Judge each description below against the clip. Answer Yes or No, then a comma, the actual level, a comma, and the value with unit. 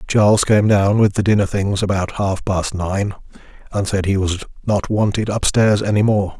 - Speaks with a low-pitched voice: Yes, low, 100 Hz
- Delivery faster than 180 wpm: Yes, average, 190 wpm